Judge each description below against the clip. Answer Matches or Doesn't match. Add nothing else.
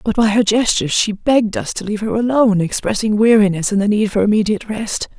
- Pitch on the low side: Doesn't match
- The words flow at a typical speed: Doesn't match